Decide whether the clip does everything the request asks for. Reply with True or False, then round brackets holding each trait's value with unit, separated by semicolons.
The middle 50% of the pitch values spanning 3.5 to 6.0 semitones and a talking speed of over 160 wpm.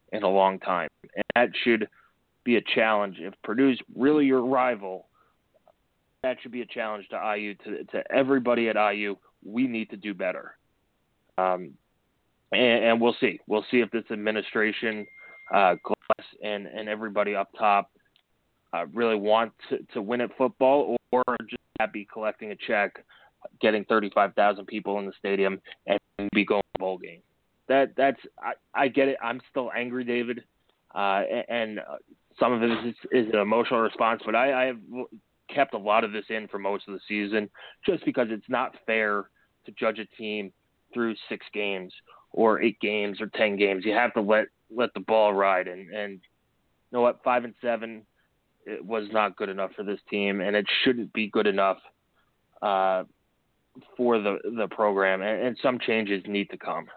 False (3.0 semitones; 180 wpm)